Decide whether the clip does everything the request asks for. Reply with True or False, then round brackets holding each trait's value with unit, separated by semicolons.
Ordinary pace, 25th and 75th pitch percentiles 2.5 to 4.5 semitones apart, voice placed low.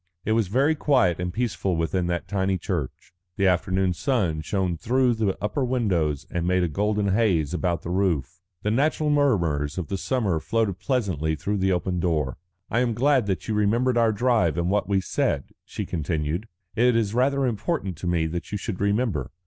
False (190 wpm; 5.0 semitones; 95 Hz)